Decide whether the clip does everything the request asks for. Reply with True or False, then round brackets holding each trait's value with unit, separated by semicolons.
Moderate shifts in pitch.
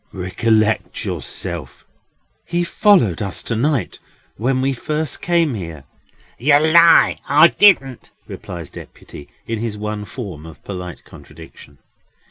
False (8.6 semitones)